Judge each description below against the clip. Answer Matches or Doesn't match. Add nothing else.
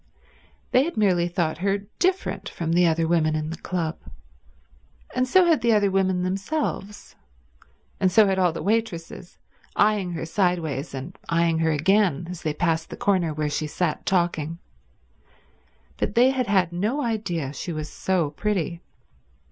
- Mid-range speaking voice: Matches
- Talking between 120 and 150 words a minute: Doesn't match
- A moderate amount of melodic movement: Matches